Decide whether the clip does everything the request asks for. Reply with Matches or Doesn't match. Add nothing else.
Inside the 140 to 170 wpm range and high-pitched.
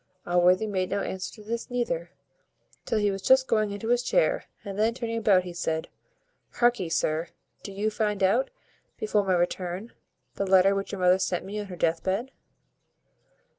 Doesn't match